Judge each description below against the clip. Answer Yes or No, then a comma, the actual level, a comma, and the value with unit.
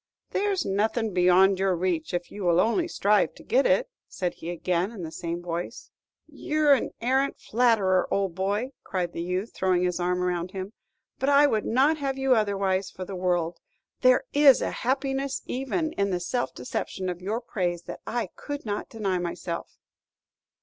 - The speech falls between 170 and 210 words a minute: Yes, average, 180 wpm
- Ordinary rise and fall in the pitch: No, wide, 6.2 semitones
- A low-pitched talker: No, high, 195 Hz